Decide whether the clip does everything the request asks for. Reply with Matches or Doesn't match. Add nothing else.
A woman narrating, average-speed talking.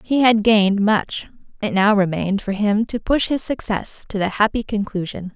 Matches